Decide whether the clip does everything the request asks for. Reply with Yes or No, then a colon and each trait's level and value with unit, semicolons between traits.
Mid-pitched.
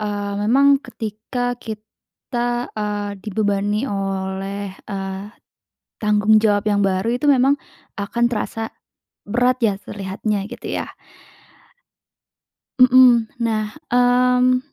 No: high, 215 Hz